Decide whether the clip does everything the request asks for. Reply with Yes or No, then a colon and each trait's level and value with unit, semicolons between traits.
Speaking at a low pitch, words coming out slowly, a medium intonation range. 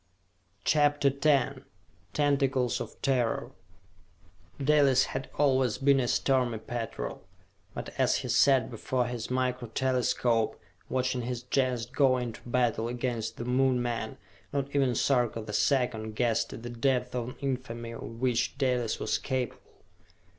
No: low, 125 Hz; slow, 130 wpm; narrow, 2.1 semitones